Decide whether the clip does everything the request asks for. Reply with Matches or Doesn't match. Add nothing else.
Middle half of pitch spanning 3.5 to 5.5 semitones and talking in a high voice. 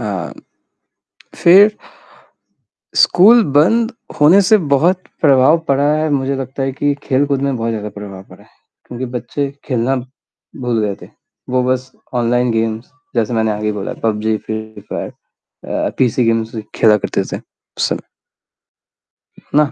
Doesn't match